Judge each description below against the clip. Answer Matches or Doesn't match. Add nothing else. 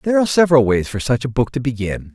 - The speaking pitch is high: Doesn't match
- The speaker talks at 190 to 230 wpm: Doesn't match